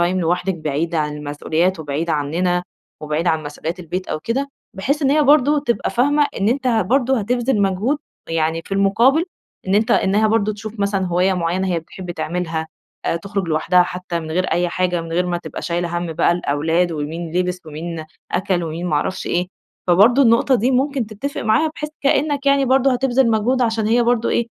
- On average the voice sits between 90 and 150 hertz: No, medium, 185 Hz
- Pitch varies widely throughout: Yes, wide, 6.1 semitones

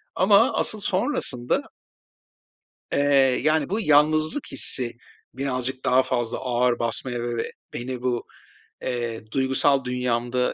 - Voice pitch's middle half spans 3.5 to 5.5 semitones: No, average, 2.8 semitones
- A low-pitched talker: Yes, low, 130 Hz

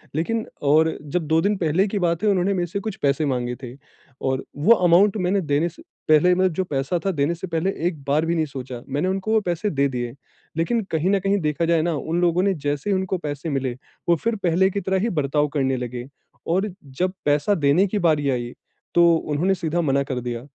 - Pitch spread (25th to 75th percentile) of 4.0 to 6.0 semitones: Yes, average, 4.7 semitones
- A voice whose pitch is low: No, medium, 165 Hz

